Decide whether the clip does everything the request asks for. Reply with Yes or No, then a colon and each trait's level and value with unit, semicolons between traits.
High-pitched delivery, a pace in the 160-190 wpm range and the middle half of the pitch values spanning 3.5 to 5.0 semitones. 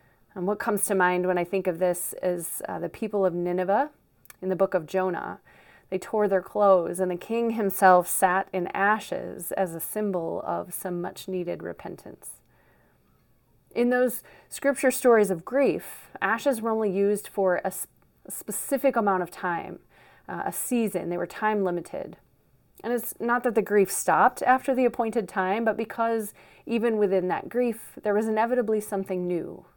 Yes: high, 200 Hz; average, 175 wpm; average, 3.8 semitones